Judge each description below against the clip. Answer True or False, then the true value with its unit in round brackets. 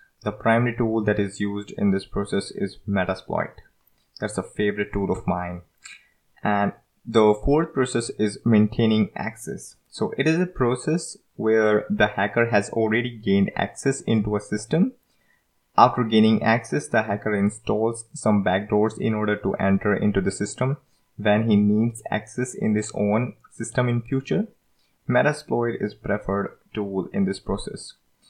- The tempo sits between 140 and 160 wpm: True (150 wpm)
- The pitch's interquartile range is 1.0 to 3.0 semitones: True (2.5 semitones)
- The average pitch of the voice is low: True (105 Hz)